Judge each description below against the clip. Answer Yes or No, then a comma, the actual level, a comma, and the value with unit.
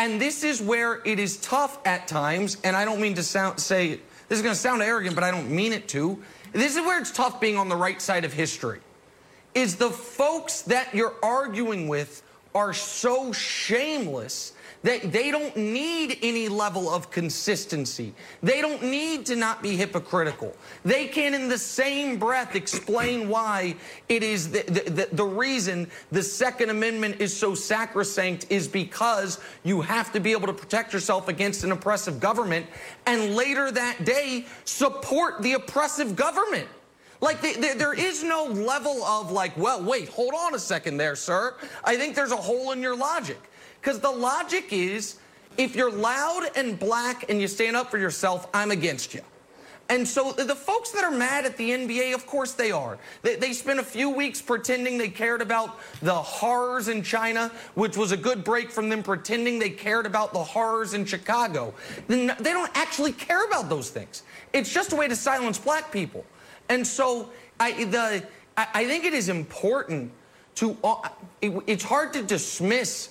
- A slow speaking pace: No, average, 185 wpm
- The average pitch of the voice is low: No, high, 230 Hz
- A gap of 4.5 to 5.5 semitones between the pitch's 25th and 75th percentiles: Yes, average, 4.8 semitones